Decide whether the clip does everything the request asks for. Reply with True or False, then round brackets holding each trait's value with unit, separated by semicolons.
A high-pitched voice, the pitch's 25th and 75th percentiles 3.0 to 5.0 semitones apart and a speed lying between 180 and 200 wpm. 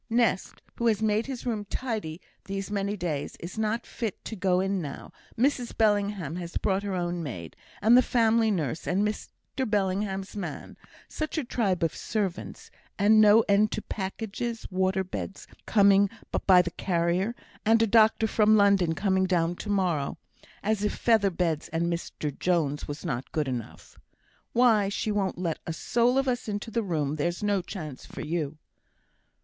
False (195 Hz; 4.0 semitones; 170 wpm)